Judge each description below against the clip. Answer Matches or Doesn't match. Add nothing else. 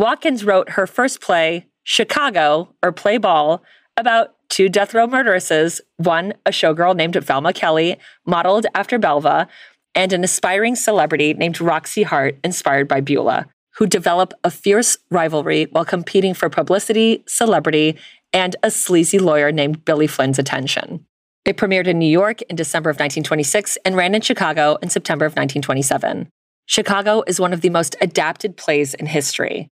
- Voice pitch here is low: Doesn't match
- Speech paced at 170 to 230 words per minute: Doesn't match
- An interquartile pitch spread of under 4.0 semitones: Doesn't match